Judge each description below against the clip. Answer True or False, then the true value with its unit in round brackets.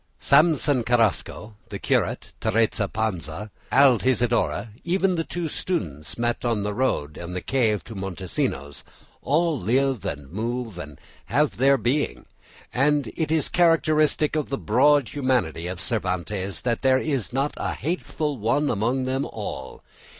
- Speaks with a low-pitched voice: True (120 Hz)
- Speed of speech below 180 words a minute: True (145 wpm)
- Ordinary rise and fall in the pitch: False (6.1 semitones)